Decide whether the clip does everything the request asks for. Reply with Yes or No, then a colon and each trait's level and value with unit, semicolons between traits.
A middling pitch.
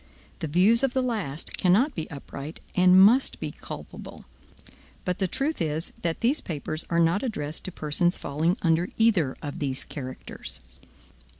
Yes: medium, 175 Hz